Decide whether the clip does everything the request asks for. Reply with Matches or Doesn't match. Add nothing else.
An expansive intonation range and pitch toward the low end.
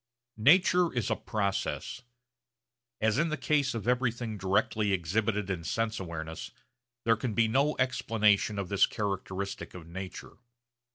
Doesn't match